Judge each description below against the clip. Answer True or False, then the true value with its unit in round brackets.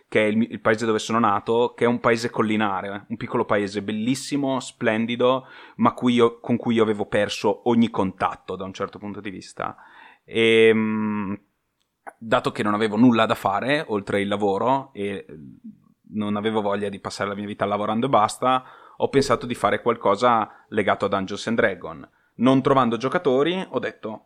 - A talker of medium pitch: False (110 Hz)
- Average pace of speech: False (175 wpm)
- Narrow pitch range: False (3.3 semitones)